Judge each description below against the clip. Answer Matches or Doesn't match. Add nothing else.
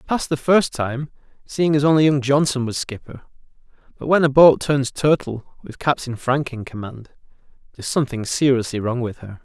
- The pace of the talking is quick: Doesn't match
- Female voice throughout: Doesn't match